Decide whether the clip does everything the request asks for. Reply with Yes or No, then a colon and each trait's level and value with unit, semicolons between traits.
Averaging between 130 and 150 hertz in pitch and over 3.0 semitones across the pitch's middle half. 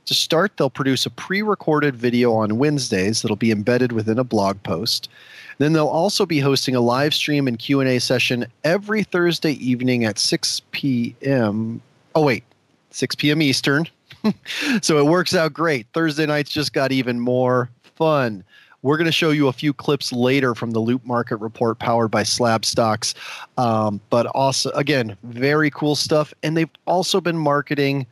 Yes: low, 135 Hz; average, 4.2 semitones